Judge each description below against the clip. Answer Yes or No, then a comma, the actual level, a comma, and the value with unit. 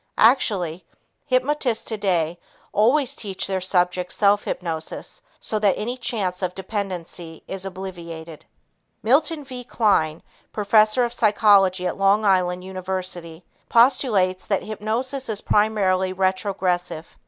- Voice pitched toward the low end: No, high, 195 Hz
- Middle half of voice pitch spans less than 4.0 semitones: Yes, average, 3.4 semitones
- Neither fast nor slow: No, slow, 115 wpm